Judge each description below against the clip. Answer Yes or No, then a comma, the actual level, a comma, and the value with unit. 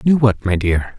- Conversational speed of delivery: No, fast, 245 wpm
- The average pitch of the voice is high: No, low, 110 Hz